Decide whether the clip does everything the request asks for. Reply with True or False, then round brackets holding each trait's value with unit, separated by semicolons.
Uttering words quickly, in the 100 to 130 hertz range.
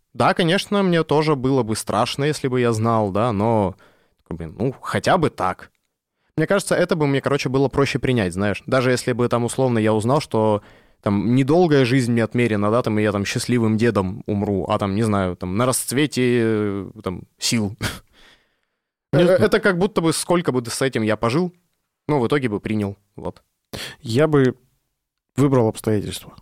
True (175 wpm; 120 Hz)